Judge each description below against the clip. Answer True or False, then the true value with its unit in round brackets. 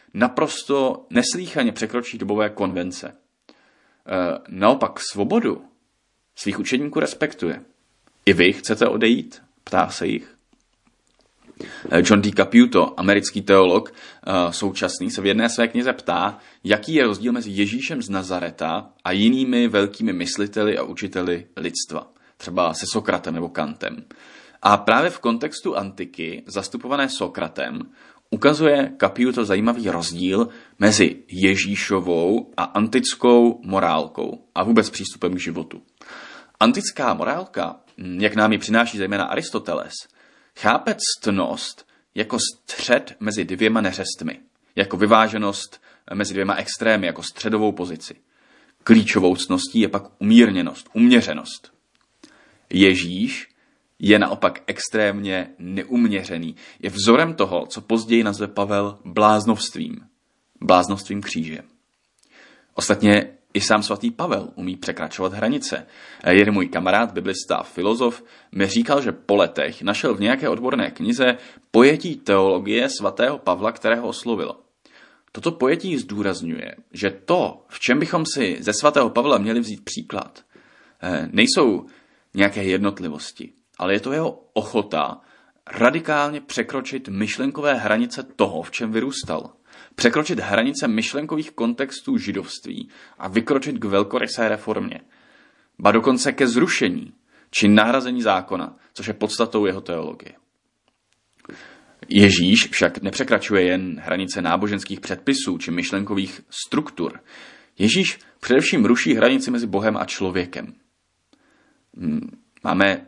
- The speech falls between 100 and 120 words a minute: True (115 wpm)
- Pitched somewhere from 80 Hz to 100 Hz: False (110 Hz)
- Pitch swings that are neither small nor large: False (5.9 semitones)